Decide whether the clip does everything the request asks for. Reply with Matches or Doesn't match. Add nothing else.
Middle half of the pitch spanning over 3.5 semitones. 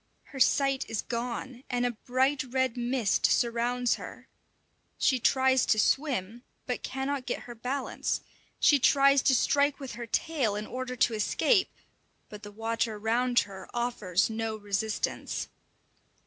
Doesn't match